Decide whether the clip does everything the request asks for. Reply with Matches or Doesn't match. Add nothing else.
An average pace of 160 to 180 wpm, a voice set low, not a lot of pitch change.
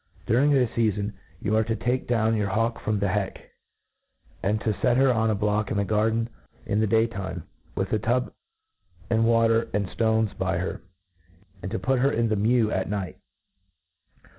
Doesn't match